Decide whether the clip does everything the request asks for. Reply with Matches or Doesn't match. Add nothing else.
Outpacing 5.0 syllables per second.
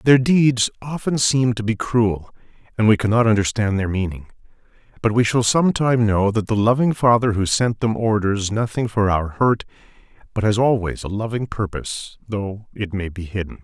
Doesn't match